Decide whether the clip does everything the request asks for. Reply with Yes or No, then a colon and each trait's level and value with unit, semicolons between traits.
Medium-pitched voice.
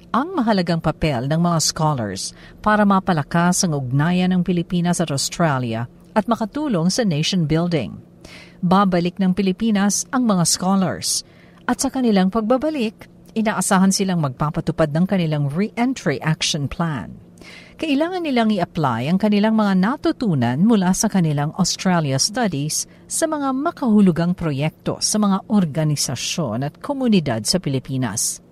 Yes: medium, 180 Hz